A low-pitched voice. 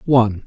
Yes: low, 115 Hz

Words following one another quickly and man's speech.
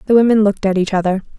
No: fast, 260 wpm; female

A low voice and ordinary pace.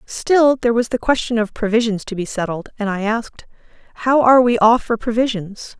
No: high, 225 Hz; average, 185 wpm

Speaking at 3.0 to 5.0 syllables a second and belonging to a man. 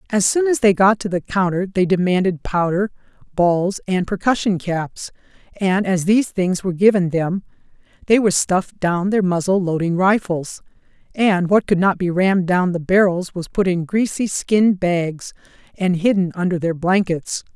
No: 4.8 syllables/s; female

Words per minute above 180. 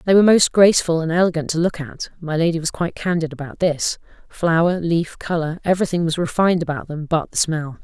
Yes: average, 200 wpm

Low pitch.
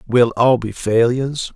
Yes: low, 120 Hz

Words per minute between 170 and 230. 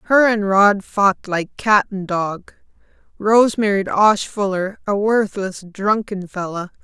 No: average, 140 wpm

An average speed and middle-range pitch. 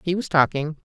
Yes: average, 195 wpm; medium, 165 Hz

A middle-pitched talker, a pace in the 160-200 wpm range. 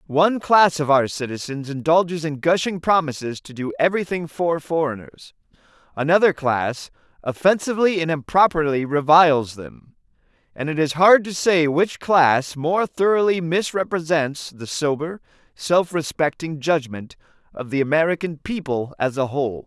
No: medium, 155 Hz; slow, 135 wpm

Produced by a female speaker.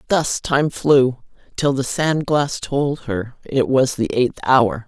Yes: female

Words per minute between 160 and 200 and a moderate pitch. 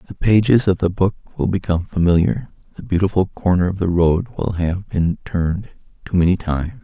No: average, 185 wpm; very low, 95 Hz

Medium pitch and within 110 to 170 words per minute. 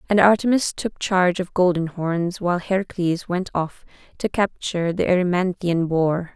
Yes: medium, 180 Hz; average, 150 wpm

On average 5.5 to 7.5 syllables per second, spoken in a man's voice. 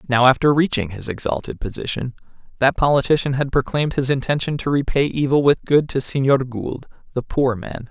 Yes: 5.6 syllables/s; male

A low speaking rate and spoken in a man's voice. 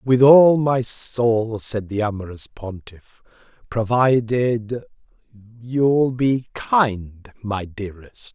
Yes: slow, 95 wpm; male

